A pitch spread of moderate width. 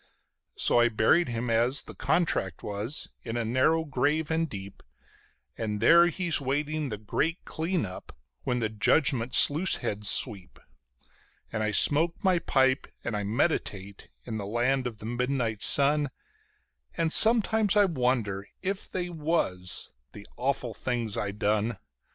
No: wide, 6.6 semitones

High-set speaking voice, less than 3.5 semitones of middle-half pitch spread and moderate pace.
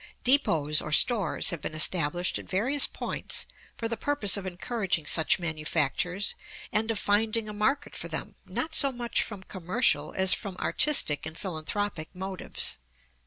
No: high, 195 Hz; wide, 5.6 semitones; average, 155 wpm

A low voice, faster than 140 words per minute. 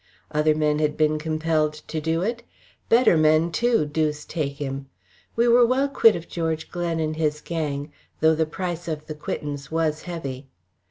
No: medium, 155 Hz; average, 175 wpm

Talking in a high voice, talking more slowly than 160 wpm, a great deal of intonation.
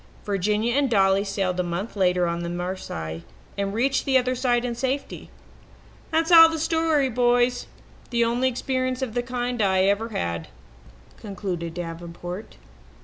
Yes: high, 225 Hz; average, 150 wpm; wide, 5.8 semitones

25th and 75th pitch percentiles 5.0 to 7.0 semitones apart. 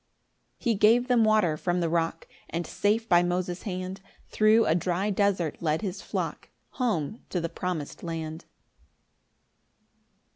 No: average, 4.1 semitones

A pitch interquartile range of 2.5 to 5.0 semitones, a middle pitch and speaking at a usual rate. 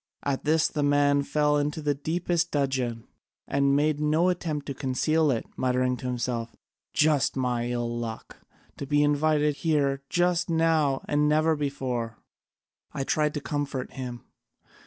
Yes: average, 2.9 semitones; medium, 145 Hz; average, 155 wpm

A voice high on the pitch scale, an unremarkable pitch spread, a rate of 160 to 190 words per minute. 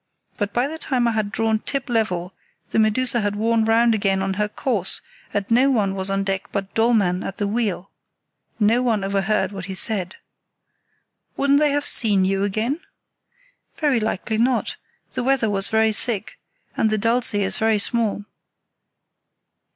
Yes: high, 215 Hz; average, 3.2 semitones; average, 165 wpm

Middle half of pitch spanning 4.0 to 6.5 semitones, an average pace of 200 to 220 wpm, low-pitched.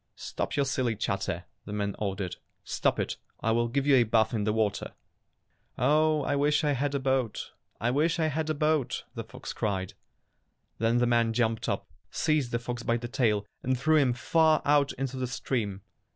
Yes: average, 4.3 semitones; fast, 205 wpm; low, 125 Hz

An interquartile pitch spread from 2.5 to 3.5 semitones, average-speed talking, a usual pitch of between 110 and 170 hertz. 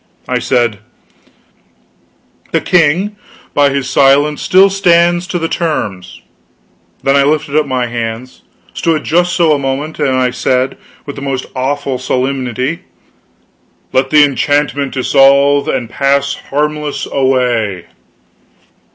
No: average, 2.8 semitones; slow, 125 wpm; medium, 140 Hz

